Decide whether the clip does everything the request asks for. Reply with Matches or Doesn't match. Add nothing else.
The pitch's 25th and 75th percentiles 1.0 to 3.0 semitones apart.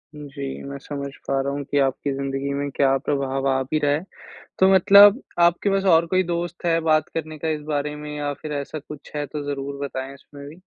Matches